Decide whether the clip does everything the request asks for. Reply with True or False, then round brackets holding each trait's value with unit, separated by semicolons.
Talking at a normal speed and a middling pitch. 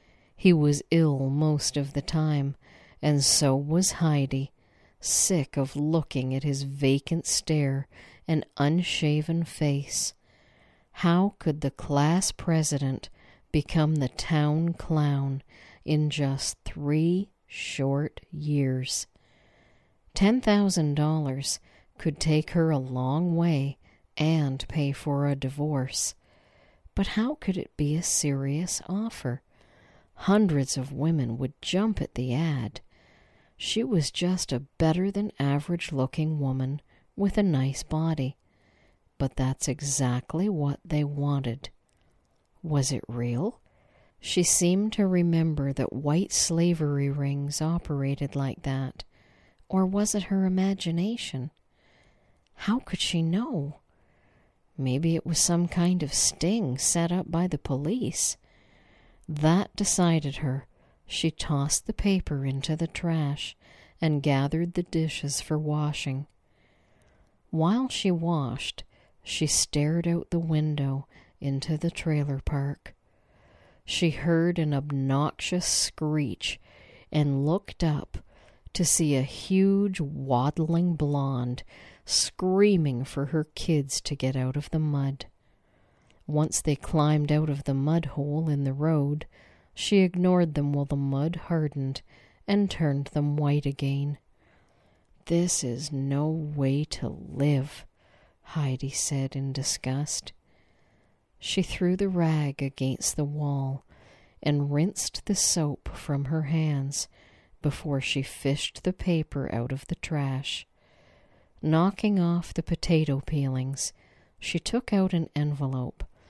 False (120 wpm; 145 Hz)